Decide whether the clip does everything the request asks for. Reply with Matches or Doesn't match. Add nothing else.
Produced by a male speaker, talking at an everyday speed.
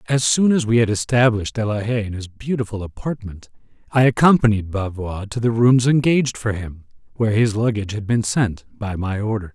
Matches